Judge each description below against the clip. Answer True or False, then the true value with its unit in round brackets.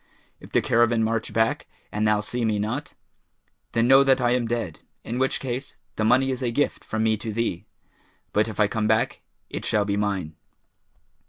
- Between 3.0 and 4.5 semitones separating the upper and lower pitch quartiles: False (2.5 semitones)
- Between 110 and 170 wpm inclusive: False (195 wpm)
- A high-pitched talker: False (115 Hz)